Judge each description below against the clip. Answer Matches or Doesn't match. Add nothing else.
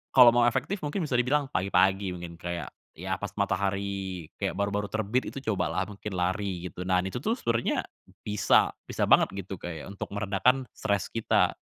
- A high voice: Doesn't match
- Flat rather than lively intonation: Doesn't match